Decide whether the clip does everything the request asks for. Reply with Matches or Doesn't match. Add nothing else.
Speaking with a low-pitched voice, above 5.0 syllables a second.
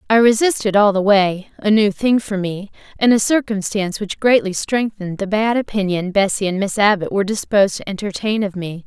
Doesn't match